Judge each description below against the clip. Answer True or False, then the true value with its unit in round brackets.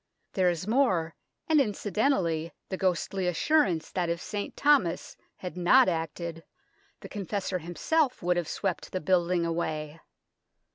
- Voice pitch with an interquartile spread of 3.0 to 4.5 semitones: True (3.5 semitones)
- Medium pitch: True (180 Hz)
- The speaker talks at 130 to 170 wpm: True (135 wpm)